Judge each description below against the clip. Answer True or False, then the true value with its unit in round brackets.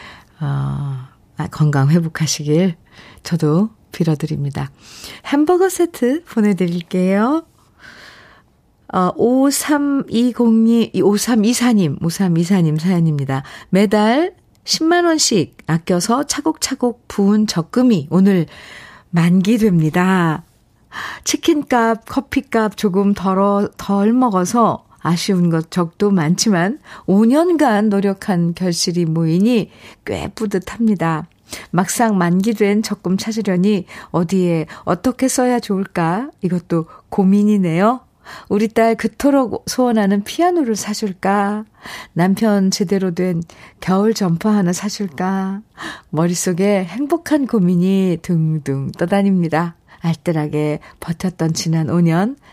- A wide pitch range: False (4.8 semitones)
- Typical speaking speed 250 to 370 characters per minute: False (220 characters per minute)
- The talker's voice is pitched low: False (195 Hz)